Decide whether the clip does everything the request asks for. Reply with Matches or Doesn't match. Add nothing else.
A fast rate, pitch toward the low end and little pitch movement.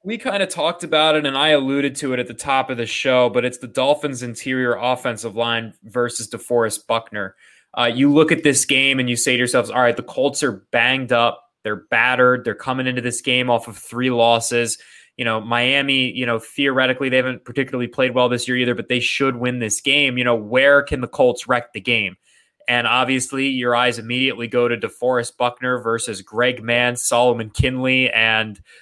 Matches